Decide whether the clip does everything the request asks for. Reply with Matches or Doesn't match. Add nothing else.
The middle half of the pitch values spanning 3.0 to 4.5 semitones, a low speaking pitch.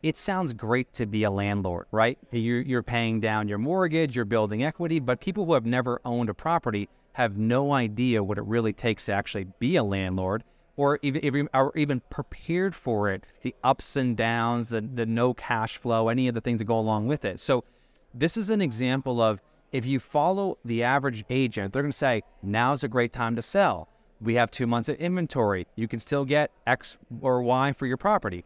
Matches